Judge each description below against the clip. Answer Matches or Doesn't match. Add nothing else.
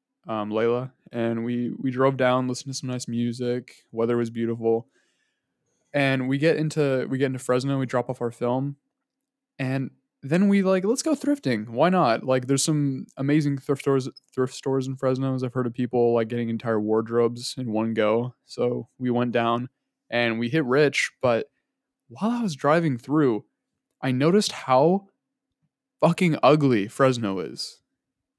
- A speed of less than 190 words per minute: Matches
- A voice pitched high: Doesn't match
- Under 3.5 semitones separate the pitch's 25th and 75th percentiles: Doesn't match